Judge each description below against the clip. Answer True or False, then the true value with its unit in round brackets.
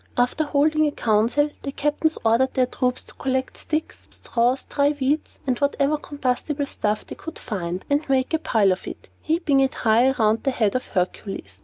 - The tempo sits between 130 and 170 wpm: False (185 wpm)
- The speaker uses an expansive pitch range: False (4.3 semitones)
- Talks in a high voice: True (260 Hz)